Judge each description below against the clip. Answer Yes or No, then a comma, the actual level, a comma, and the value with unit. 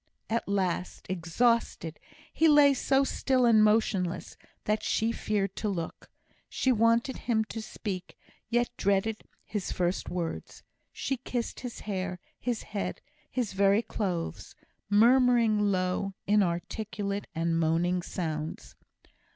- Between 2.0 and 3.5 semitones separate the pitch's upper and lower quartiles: No, average, 4.2 semitones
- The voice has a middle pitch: No, high, 205 Hz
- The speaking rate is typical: No, slow, 120 wpm